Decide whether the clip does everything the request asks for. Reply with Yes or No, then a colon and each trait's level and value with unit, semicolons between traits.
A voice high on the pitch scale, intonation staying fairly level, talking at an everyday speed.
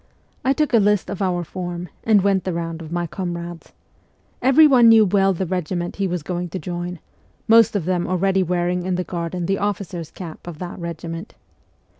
No: medium, 180 Hz; narrow, 2.2 semitones; average, 190 wpm